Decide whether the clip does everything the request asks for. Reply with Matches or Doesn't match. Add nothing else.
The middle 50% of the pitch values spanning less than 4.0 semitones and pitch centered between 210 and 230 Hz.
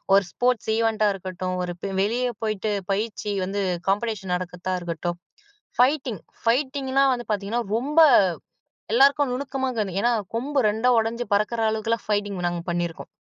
Doesn't match